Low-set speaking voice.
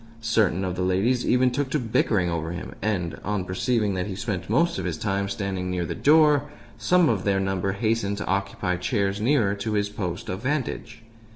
Yes: low, 100 Hz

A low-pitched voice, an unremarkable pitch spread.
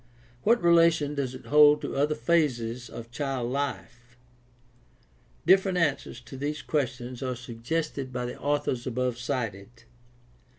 Yes: low, 130 Hz; average, 3.6 semitones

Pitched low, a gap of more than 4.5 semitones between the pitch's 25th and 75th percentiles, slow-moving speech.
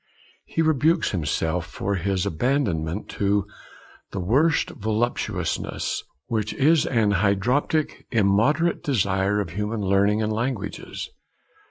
Yes: low, 105 Hz; average, 5.0 semitones; slow, 110 wpm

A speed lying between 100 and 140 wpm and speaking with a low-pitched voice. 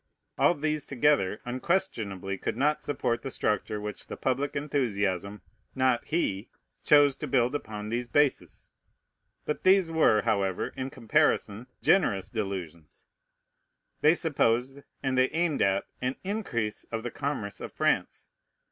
Yes: slow, 135 wpm; low, 125 Hz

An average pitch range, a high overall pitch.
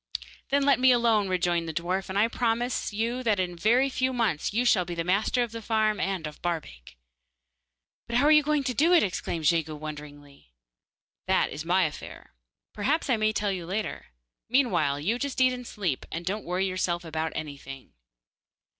No: wide, 6.4 semitones; high, 195 Hz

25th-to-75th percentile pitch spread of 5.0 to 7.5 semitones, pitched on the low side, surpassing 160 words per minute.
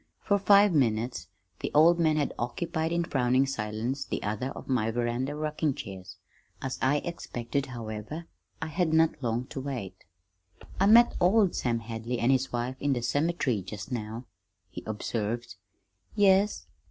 No: wide, 5.5 semitones; low, 130 Hz; average, 155 wpm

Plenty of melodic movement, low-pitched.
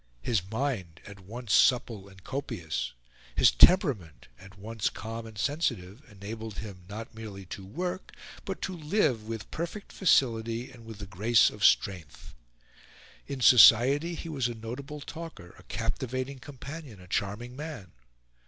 Yes: wide, 5.7 semitones; low, 115 Hz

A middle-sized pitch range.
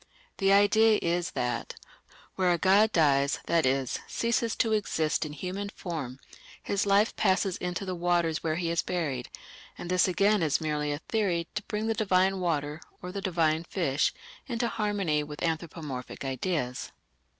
Yes: average, 4.5 semitones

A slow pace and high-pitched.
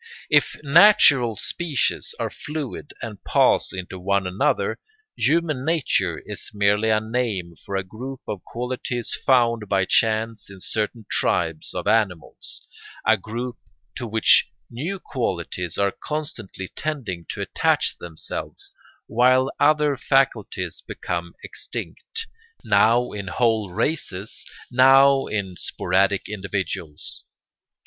No: slow, 115 wpm; low, 110 Hz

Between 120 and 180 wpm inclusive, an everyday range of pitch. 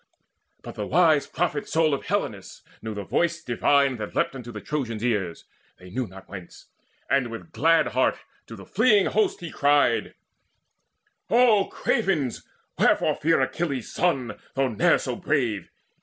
No: average, 155 wpm; wide, 6.6 semitones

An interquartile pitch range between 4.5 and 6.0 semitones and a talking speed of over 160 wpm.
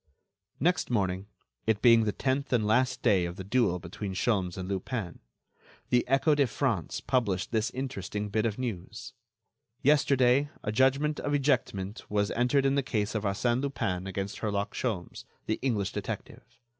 No: average, 4.9 semitones; average, 155 wpm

